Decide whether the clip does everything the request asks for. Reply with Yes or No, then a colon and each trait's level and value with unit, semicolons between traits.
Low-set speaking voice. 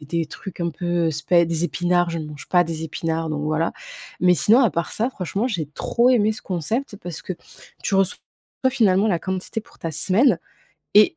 No: medium, 175 Hz